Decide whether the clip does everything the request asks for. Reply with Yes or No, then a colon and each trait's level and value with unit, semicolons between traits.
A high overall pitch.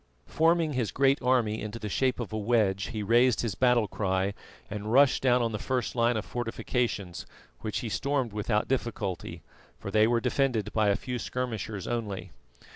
No: low, 115 Hz